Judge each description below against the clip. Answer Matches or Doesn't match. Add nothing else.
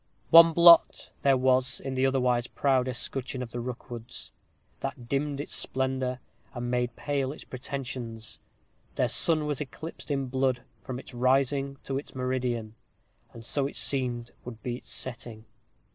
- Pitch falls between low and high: Doesn't match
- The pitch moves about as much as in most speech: Doesn't match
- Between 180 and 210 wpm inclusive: Doesn't match